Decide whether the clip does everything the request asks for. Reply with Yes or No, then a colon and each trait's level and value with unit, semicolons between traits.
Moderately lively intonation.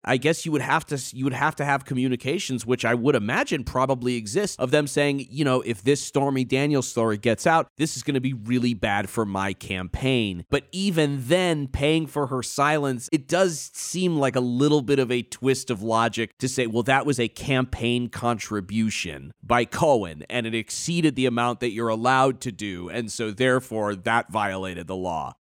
Yes: average, 3.8 semitones